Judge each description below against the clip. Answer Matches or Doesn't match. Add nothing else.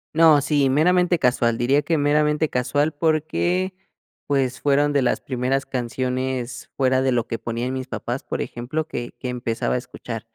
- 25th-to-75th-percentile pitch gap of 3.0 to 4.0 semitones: Matches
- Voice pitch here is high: Doesn't match